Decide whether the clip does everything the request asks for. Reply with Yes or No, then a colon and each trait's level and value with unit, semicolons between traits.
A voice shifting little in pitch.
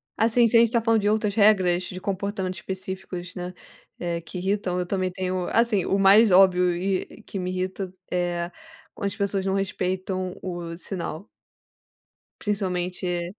Yes: narrow, 1.9 semitones